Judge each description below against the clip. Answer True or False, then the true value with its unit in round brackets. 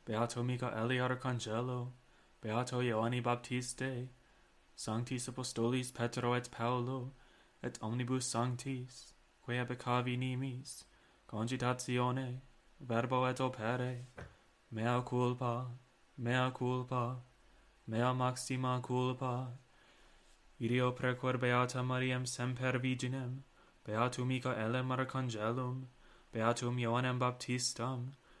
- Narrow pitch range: True (1.0 semitones)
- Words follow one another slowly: True (90 wpm)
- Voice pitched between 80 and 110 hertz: False (125 Hz)